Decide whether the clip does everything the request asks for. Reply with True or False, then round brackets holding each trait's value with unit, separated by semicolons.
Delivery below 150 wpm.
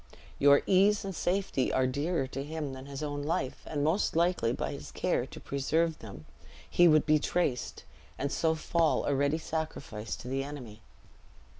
False (175 wpm)